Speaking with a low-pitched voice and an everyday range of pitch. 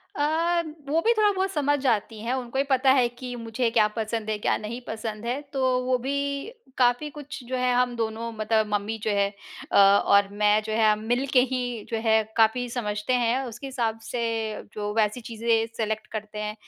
No: high, 235 Hz; average, 3.2 semitones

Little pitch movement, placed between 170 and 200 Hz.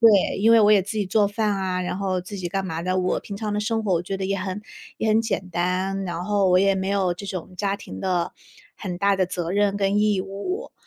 Yes: narrow, 2.0 semitones; high, 195 Hz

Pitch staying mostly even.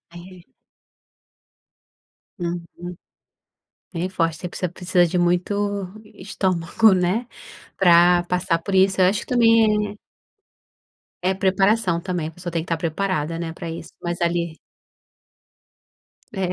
Yes: narrow, 2.2 semitones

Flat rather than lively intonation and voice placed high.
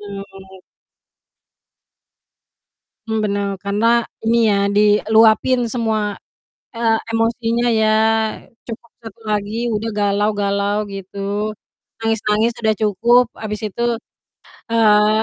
Yes: narrow, 1.9 semitones; high, 215 Hz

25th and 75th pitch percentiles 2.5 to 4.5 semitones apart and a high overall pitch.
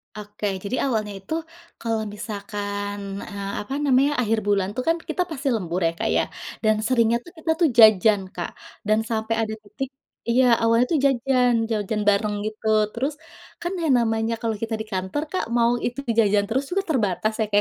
Yes: average, 3.4 semitones; high, 220 Hz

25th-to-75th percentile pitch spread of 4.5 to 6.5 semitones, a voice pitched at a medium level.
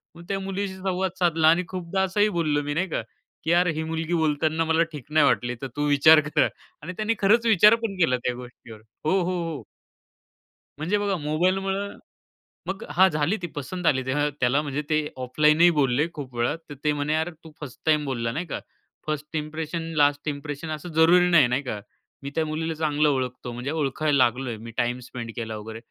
No: average, 3.9 semitones; medium, 155 Hz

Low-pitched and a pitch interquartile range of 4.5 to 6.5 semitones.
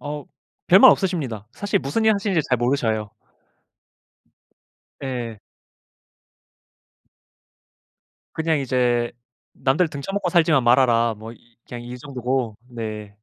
Yes: low, 130 Hz; average, 5.3 semitones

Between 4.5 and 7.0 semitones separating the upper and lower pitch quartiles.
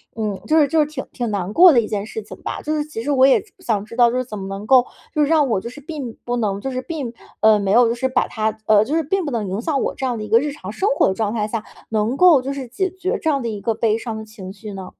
Yes: average, 5.1 semitones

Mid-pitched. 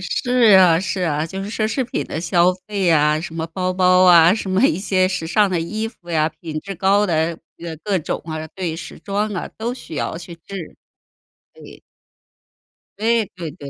Yes: medium, 180 Hz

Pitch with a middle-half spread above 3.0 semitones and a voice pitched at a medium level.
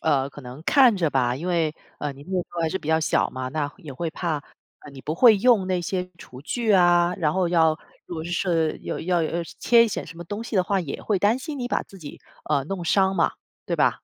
Yes: average, 3.8 semitones; medium, 175 Hz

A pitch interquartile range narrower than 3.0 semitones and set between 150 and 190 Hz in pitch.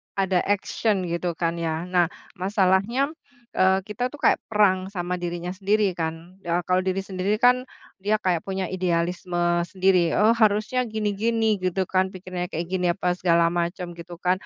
Yes: narrow, 2.6 semitones; medium, 185 Hz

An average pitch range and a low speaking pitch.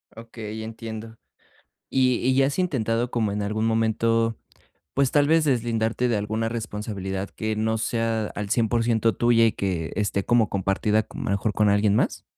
No: narrow, 1.9 semitones; low, 110 Hz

